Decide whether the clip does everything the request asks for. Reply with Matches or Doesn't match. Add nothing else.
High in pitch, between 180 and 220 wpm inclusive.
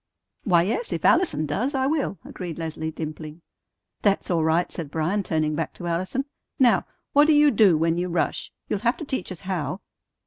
Doesn't match